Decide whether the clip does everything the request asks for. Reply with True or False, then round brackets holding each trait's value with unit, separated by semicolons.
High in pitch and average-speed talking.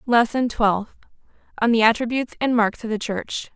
True (230 Hz; 170 wpm)